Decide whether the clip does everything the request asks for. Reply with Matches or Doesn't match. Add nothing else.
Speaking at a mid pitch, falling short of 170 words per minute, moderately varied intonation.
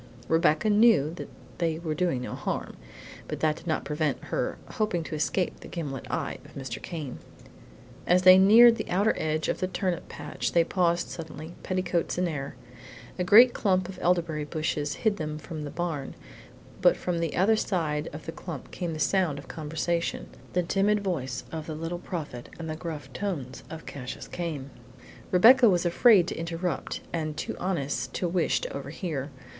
Doesn't match